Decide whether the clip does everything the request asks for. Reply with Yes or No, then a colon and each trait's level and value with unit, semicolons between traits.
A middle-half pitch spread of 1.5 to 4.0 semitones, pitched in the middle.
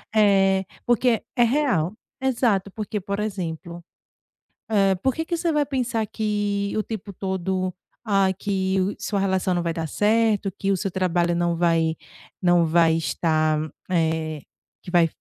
No: average, 3.7 semitones; high, 195 Hz